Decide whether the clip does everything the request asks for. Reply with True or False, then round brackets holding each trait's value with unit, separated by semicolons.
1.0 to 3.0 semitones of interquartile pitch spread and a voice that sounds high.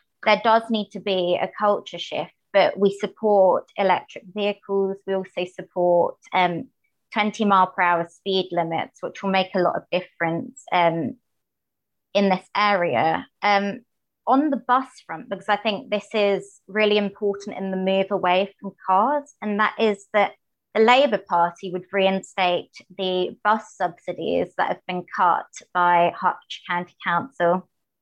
True (2.5 semitones; 195 Hz)